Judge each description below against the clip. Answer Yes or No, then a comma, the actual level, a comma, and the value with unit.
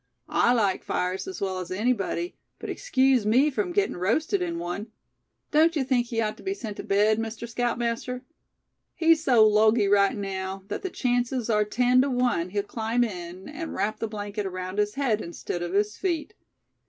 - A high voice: Yes, high, 225 Hz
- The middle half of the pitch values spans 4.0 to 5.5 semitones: Yes, average, 4.3 semitones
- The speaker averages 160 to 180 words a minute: No, average, 190 wpm